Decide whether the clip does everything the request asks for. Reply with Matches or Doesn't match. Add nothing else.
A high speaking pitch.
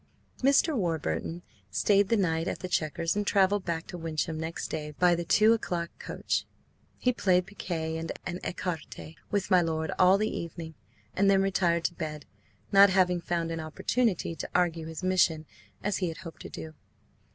Doesn't match